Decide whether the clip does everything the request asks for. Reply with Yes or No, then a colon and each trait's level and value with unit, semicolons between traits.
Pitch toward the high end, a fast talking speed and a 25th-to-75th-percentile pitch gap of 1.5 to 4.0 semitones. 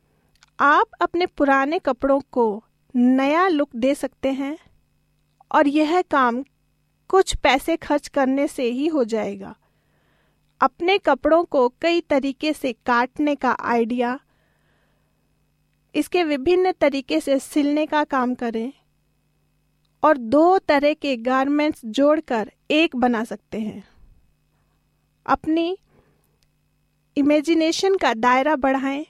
No: very high, 285 Hz; slow, 110 wpm; average, 3.5 semitones